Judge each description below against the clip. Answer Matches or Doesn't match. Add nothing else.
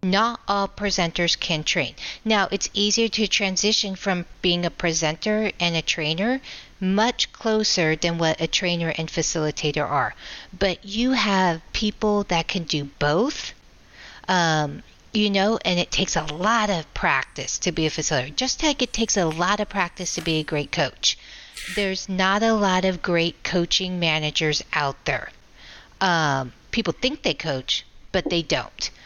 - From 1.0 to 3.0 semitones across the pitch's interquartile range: Doesn't match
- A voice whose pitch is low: Doesn't match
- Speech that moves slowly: Doesn't match